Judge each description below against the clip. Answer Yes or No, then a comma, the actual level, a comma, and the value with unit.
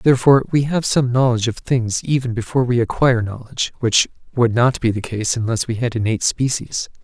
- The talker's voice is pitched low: Yes, low, 120 Hz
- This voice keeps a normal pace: Yes, average, 195 wpm